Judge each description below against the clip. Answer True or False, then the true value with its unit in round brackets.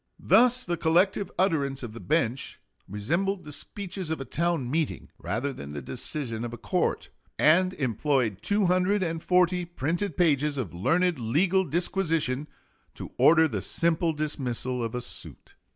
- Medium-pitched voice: True (155 Hz)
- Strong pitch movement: True (6.0 semitones)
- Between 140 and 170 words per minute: True (145 wpm)